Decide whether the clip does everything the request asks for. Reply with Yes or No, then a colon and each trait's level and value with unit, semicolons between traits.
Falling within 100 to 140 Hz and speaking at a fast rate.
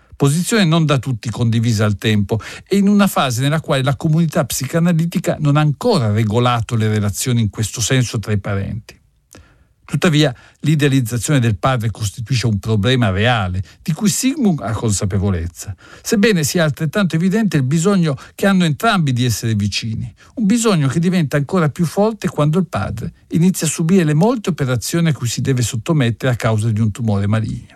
Yes: low, 135 Hz; fast, 175 wpm